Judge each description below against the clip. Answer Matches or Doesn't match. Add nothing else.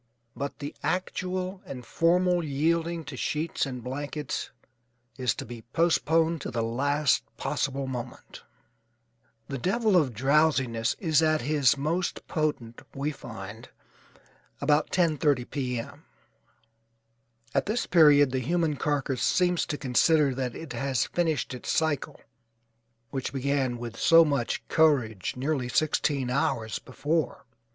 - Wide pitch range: Doesn't match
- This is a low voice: Doesn't match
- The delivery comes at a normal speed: Doesn't match